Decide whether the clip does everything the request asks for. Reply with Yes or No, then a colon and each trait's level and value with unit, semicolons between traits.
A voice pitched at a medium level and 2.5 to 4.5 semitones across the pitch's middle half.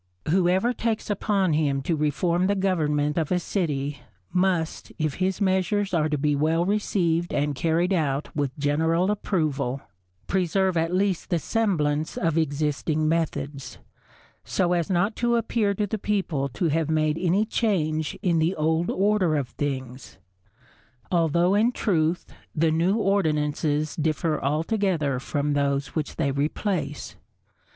Yes: medium, 165 Hz; average, 4.1 semitones